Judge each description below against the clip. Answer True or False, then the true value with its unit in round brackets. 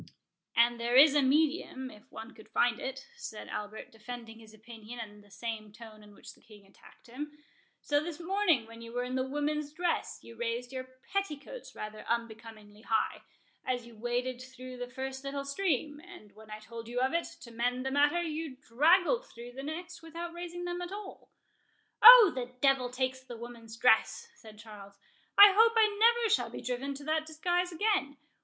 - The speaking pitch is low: False (255 Hz)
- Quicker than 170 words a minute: True (190 wpm)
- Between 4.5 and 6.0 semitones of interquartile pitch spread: True (5.6 semitones)